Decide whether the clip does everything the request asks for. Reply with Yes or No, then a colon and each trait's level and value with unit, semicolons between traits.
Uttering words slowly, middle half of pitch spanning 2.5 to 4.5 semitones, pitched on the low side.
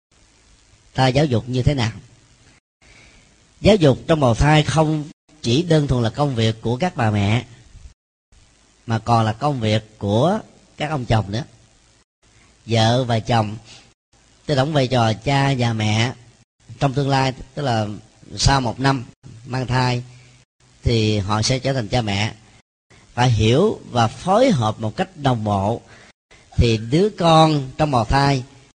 Yes: slow, 155 wpm; average, 3.7 semitones; low, 120 Hz